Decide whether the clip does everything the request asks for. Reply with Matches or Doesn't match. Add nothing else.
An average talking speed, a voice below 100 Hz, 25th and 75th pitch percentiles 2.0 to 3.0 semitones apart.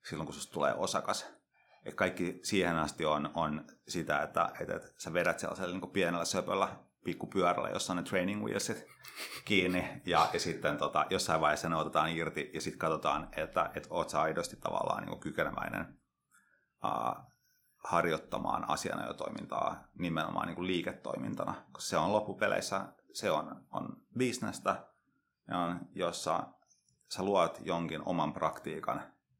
Matches